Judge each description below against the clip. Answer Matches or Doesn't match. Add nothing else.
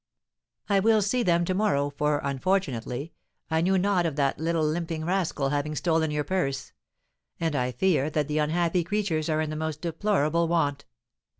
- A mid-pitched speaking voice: Matches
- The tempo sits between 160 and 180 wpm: Matches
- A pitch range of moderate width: Matches